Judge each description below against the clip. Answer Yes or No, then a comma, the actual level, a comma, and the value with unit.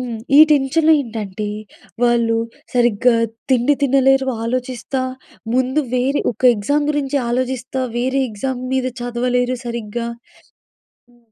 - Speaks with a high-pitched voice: Yes, very high, 250 Hz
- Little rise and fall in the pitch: Yes, narrow, 2.0 semitones